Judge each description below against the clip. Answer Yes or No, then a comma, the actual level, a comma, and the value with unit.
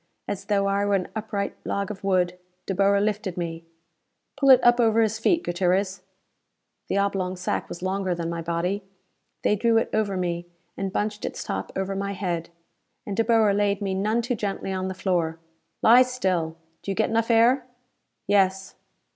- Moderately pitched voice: No, high, 195 Hz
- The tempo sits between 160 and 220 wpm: Yes, average, 185 wpm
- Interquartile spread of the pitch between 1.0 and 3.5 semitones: Yes, average, 2.7 semitones